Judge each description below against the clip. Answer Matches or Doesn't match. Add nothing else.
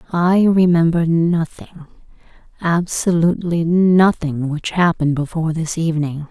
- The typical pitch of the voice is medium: Matches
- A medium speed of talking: Doesn't match